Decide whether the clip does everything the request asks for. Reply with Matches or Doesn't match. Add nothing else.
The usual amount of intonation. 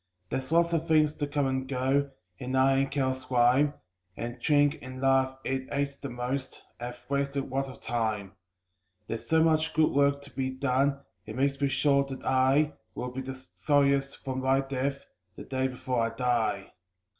Doesn't match